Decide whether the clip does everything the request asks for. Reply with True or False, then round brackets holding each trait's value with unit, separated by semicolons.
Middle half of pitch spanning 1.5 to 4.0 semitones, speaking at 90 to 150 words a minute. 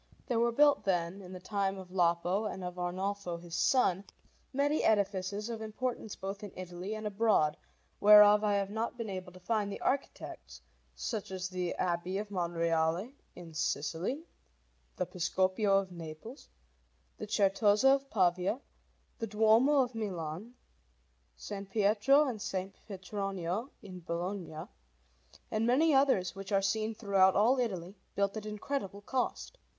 True (3.3 semitones; 145 wpm)